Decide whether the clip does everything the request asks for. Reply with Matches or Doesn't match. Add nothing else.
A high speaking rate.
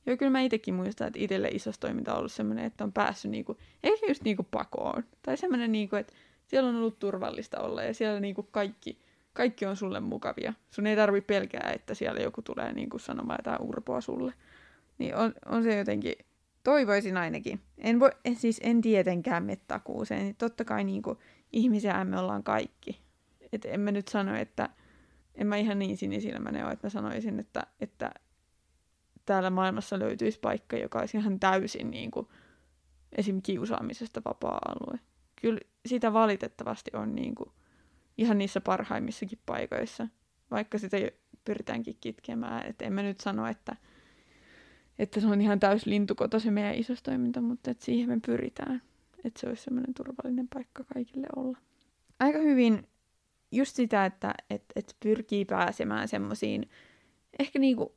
Matches